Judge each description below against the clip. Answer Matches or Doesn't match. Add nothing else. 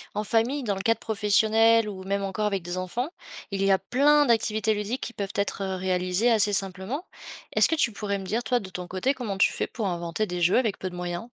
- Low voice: Doesn't match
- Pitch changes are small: Doesn't match